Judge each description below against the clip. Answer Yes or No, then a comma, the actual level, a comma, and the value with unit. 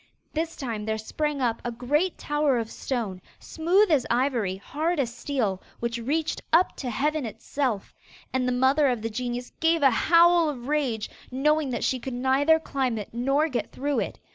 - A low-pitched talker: No, very high, 265 Hz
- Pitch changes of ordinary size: Yes, average, 4.2 semitones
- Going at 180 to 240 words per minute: Yes, average, 185 wpm